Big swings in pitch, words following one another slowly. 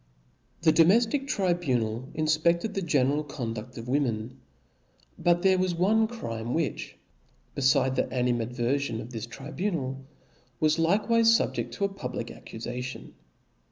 Yes: wide, 6.6 semitones; slow, 130 wpm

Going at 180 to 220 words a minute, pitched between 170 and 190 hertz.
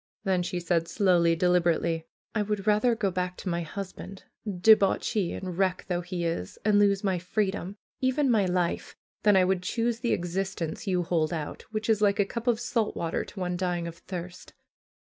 Yes: average, 195 wpm; medium, 185 Hz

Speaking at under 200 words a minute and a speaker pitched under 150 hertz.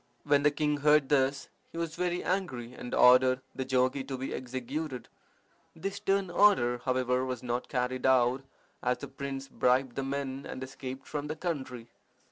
Yes: average, 170 wpm; low, 135 Hz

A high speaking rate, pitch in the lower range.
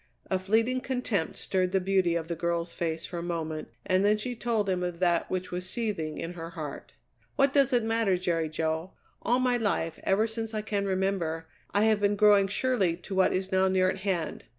No: fast, 215 wpm; high, 190 Hz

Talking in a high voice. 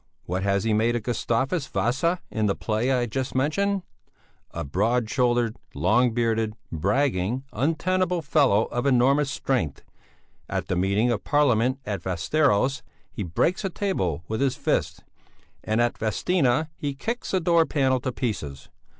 No: low, 125 Hz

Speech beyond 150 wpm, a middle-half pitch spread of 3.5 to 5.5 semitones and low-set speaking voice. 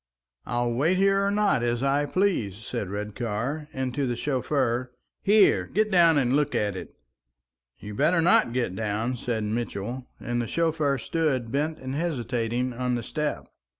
Yes: average, 165 wpm; average, 4.8 semitones; low, 130 Hz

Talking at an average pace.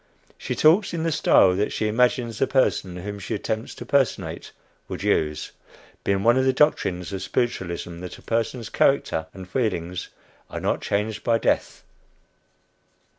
Yes: average, 160 wpm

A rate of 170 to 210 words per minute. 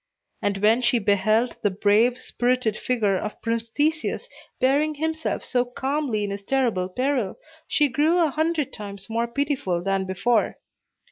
No: average, 150 wpm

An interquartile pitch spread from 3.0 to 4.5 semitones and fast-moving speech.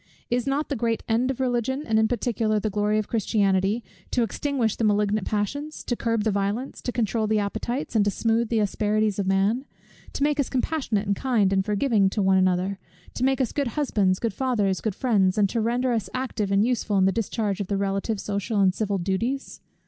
Yes: average, 3.4 semitones; fast, 215 wpm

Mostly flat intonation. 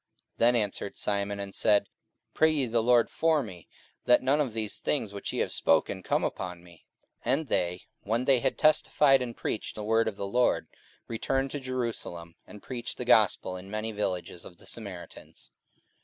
No: average, 4.3 semitones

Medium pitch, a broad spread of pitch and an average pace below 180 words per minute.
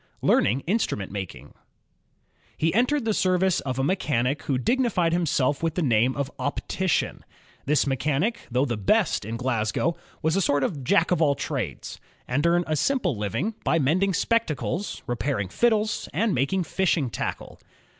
Yes: medium, 155 Hz; wide, 6.5 semitones; average, 165 wpm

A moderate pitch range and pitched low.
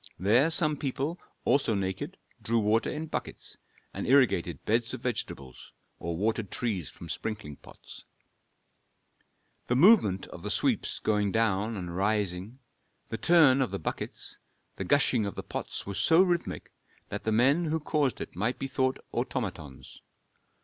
No: wide, 5.8 semitones; low, 115 Hz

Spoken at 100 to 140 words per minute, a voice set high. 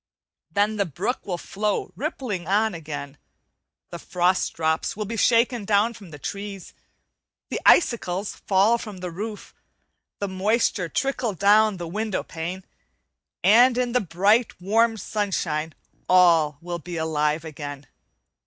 Yes: slow, 135 wpm; high, 195 Hz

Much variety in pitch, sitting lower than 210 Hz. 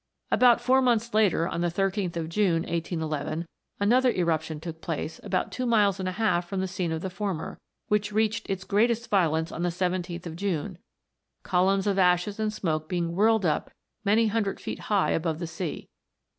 No: average, 3.8 semitones; medium, 185 Hz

